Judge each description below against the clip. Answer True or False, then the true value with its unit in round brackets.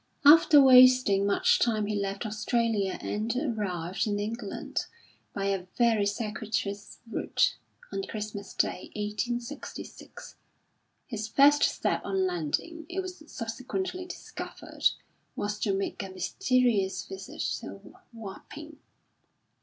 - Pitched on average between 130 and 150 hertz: False (215 Hz)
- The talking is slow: True (115 wpm)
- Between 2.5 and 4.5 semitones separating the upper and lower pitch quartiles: True (4.2 semitones)